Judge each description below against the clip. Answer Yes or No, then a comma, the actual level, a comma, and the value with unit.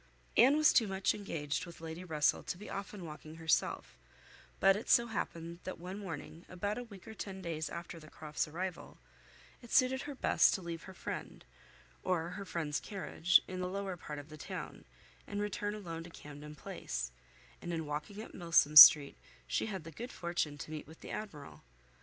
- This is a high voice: No, medium, 175 Hz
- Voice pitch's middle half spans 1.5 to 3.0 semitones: No, average, 4.3 semitones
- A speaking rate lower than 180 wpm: No, average, 195 wpm